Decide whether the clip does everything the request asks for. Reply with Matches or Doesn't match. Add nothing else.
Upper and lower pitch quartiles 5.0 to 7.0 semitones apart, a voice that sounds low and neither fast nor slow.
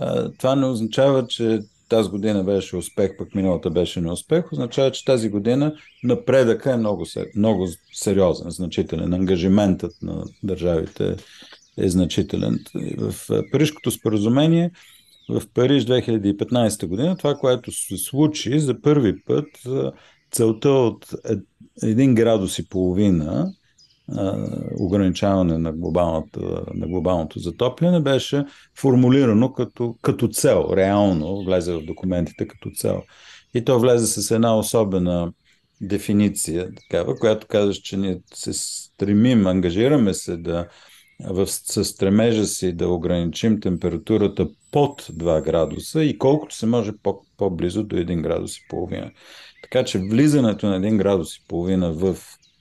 Matches